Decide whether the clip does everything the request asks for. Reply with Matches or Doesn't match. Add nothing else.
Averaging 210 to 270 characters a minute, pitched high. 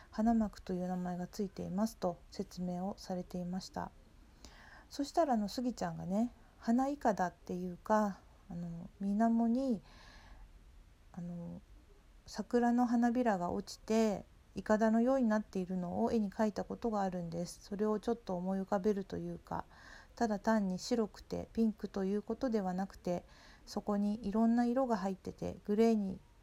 Doesn't match